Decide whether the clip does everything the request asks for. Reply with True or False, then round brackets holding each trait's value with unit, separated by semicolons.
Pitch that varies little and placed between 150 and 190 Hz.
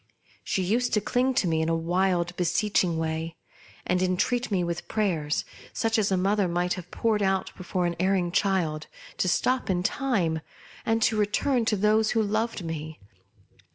False (3.9 semitones; 185 Hz)